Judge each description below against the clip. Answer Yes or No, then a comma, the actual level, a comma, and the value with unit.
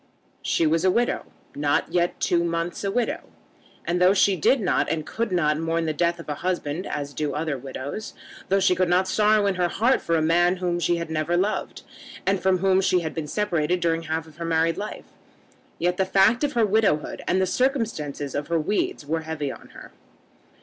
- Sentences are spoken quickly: Yes, fast, 210 wpm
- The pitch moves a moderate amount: Yes, average, 3.3 semitones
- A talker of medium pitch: Yes, medium, 175 Hz